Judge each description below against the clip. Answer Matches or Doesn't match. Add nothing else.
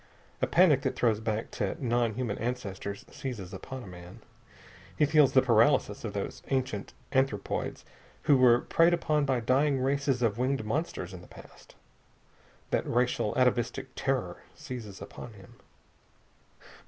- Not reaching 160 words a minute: Matches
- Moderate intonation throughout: Matches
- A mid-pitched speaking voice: Doesn't match